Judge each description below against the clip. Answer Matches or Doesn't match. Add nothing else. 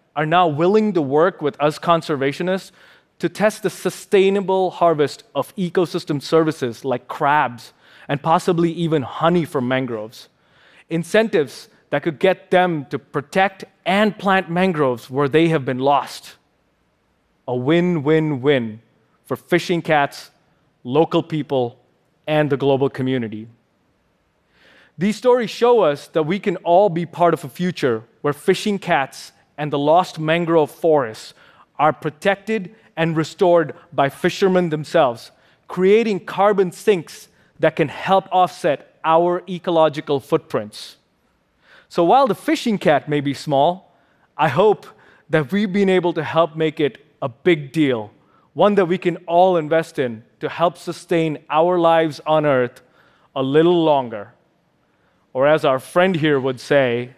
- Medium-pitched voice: Matches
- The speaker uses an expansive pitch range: Doesn't match